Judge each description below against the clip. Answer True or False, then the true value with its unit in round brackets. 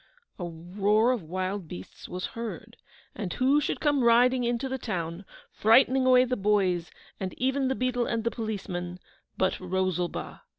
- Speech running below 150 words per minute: False (155 wpm)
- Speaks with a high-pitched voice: True (215 Hz)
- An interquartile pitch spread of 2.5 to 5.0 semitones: False (5.5 semitones)